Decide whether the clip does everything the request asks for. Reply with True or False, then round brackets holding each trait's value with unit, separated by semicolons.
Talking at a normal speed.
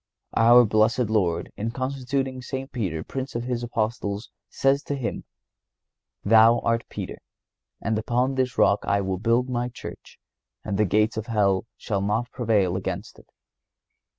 True (150 wpm)